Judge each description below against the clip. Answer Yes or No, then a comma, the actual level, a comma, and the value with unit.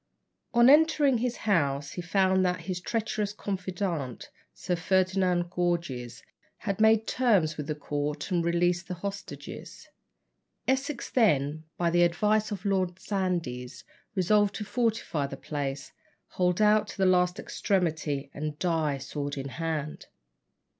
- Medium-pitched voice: Yes, medium, 180 Hz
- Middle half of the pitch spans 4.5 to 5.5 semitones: Yes, average, 5.2 semitones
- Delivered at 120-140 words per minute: Yes, slow, 135 wpm